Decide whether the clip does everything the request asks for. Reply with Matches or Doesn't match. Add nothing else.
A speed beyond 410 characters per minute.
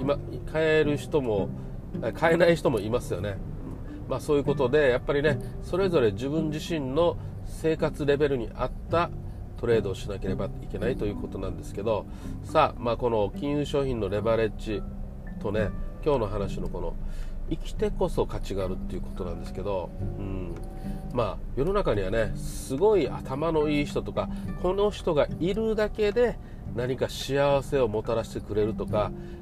Doesn't match